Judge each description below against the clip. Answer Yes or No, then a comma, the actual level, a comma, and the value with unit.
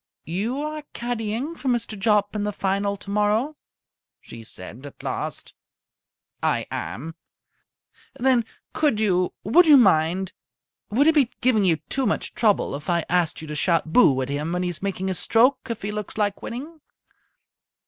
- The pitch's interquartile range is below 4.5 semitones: No, wide, 5.5 semitones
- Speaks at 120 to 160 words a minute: No, average, 170 wpm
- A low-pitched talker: No, high, 210 Hz